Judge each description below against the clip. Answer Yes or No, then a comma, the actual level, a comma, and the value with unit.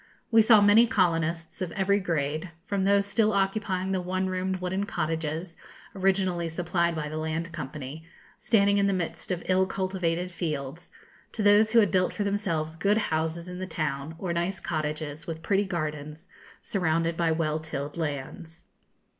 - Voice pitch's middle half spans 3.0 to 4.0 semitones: Yes, average, 3.3 semitones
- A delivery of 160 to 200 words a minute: Yes, average, 165 wpm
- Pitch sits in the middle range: Yes, medium, 175 Hz